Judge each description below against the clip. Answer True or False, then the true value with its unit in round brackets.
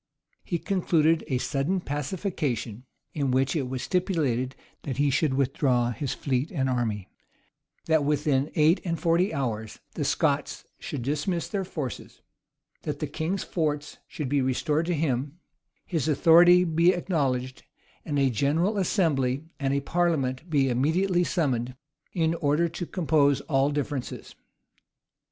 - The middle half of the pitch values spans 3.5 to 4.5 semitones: True (4.1 semitones)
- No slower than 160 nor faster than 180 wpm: False (140 wpm)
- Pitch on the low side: False (145 Hz)